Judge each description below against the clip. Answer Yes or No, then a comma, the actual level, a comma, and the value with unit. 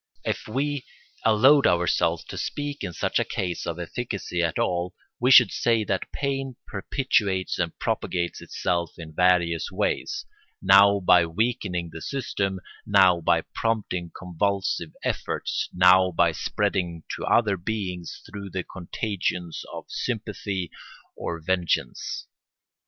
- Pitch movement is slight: No, average, 3.7 semitones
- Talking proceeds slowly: Yes, slow, 130 wpm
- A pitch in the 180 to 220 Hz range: No, very low, 95 Hz